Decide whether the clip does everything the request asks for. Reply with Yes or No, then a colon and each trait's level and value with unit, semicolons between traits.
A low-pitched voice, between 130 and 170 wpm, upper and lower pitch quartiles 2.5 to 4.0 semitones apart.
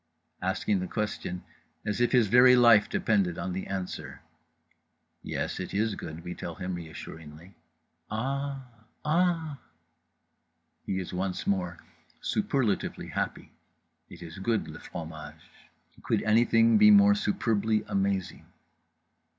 No: low, 105 Hz; slow, 135 wpm; average, 5.1 semitones